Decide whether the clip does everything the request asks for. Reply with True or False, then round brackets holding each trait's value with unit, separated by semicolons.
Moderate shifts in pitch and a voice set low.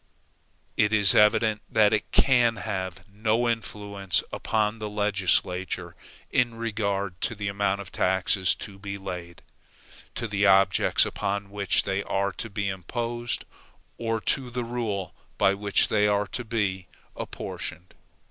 False (2.3 semitones; 100 Hz)